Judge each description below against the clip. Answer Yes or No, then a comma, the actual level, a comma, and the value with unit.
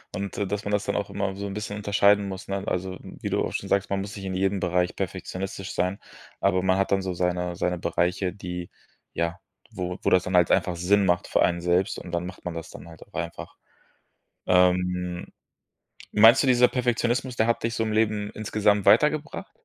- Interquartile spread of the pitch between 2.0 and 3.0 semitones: Yes, narrow, 2.4 semitones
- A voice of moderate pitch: No, very low, 95 Hz